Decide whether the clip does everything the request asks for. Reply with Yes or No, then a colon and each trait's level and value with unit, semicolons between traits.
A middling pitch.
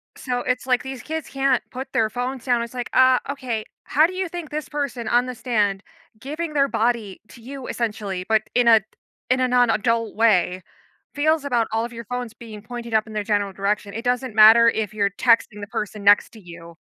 No: high, 235 Hz